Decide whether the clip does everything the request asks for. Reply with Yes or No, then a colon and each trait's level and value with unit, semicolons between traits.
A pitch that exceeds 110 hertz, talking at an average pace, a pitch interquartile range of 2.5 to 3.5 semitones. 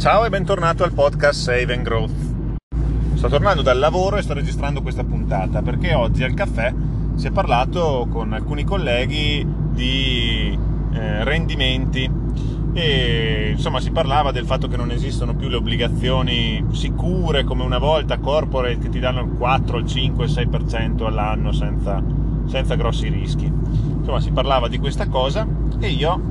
Yes: medium, 140 Hz; average, 155 wpm; average, 2.8 semitones